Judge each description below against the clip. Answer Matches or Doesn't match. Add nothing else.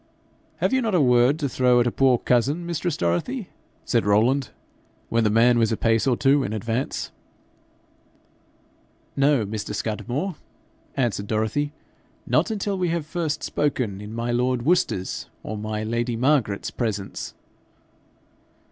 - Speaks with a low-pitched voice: Matches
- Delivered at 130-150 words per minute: Matches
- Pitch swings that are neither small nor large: Matches